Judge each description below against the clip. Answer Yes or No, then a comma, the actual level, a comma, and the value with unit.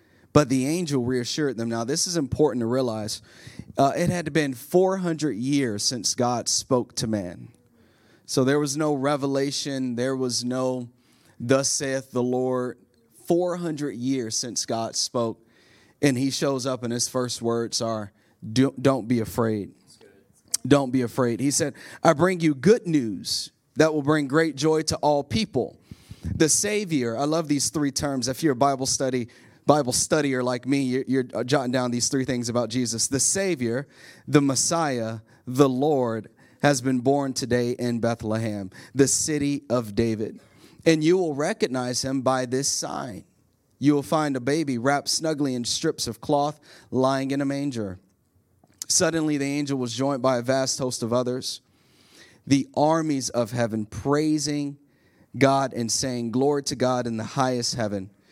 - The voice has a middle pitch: No, low, 130 Hz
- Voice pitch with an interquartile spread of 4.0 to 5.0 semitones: No, average, 3.4 semitones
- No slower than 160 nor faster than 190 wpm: Yes, average, 165 wpm